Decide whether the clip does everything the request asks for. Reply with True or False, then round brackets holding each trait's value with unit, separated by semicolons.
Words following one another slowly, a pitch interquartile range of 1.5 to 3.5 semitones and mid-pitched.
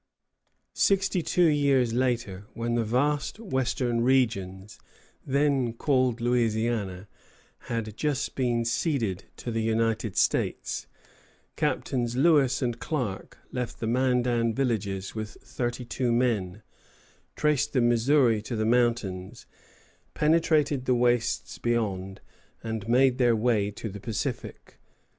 False (115 wpm; 2.8 semitones; 120 Hz)